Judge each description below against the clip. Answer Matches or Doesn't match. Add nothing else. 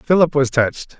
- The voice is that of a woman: Doesn't match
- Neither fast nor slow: Matches